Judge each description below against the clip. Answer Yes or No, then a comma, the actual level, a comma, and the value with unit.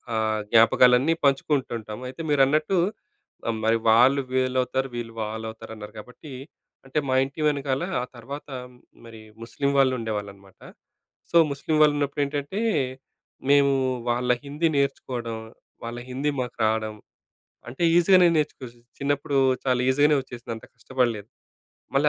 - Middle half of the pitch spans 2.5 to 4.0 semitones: Yes, average, 3.7 semitones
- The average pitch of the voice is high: No, low, 130 Hz